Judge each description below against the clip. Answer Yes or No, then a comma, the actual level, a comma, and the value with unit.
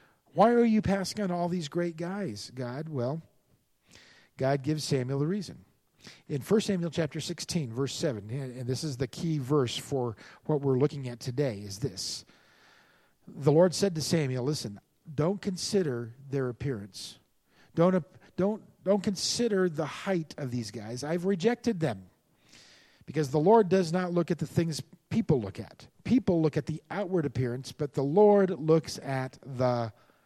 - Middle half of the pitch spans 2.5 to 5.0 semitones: No, wide, 5.6 semitones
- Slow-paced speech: No, average, 165 wpm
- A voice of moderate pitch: Yes, medium, 155 Hz